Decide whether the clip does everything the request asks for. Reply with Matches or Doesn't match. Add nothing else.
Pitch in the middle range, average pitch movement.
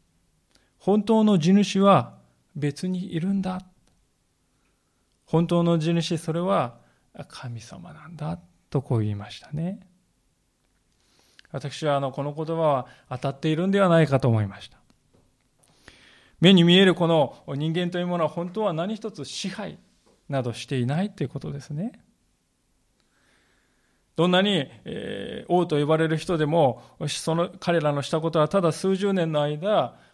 Matches